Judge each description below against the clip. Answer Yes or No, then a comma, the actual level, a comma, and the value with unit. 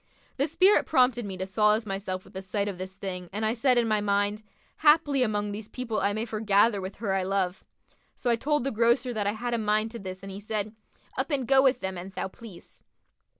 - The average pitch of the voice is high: Yes, high, 215 Hz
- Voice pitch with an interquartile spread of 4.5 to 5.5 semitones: No, average, 3.6 semitones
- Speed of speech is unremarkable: No, fast, 235 wpm